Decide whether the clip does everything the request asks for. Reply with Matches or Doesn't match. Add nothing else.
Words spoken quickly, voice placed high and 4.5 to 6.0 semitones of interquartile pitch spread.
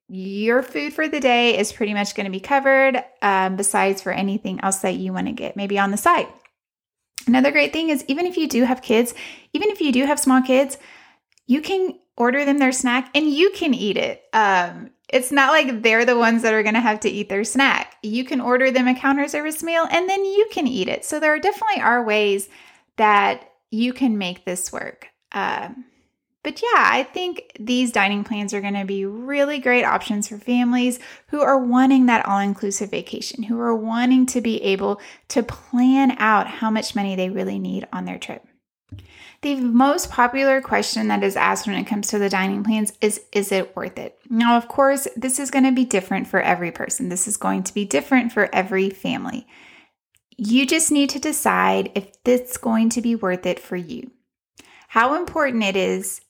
Matches